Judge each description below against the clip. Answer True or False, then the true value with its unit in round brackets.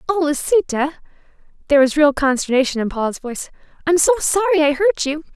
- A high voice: True (305 Hz)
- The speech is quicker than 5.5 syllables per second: True (6.1 syllables/s)